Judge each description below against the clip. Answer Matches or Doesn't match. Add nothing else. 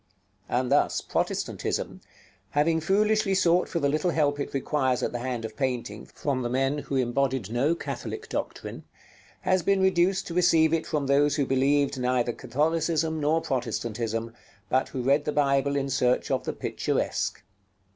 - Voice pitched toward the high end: Doesn't match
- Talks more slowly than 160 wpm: Doesn't match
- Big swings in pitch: Doesn't match